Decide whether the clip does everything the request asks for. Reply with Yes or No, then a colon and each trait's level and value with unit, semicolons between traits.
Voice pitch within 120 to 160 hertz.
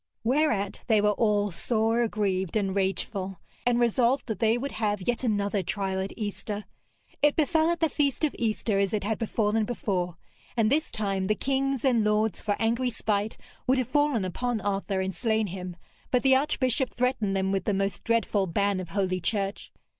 No: high, 215 Hz